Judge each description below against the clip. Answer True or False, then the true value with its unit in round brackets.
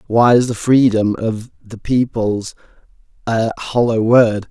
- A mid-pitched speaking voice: False (115 Hz)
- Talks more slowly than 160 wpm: True (135 wpm)